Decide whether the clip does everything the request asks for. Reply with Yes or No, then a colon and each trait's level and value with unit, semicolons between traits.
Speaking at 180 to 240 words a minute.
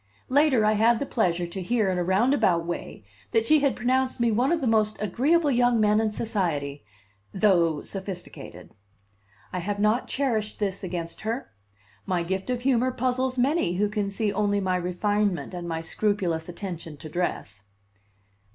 No: average, 170 wpm